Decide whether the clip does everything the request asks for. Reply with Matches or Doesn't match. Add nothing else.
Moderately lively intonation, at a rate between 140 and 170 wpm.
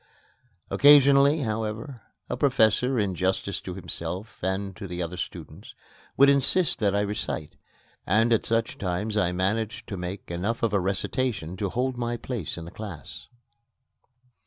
Matches